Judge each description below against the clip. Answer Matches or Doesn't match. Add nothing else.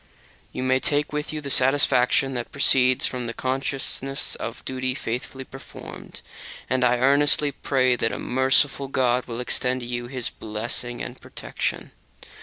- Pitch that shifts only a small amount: Matches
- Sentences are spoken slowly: Doesn't match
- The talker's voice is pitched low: Matches